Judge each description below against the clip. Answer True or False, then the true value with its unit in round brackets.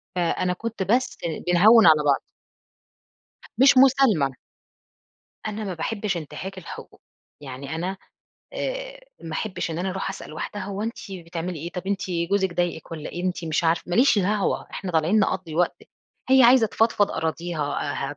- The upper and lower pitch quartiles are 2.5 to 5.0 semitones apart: True (4.3 semitones)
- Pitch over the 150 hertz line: True (185 Hz)